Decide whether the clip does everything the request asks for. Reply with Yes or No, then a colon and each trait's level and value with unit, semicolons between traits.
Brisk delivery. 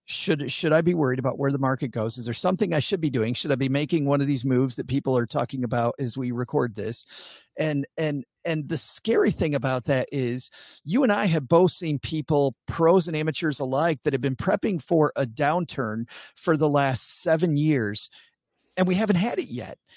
Yes: fast, 215 wpm